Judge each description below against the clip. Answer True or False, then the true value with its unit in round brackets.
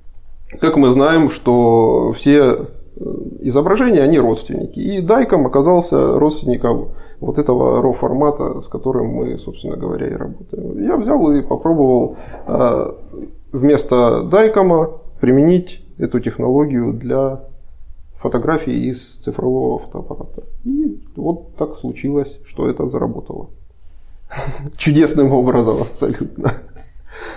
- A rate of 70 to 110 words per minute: True (105 wpm)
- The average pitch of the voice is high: False (135 Hz)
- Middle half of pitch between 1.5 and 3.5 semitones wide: False (5.4 semitones)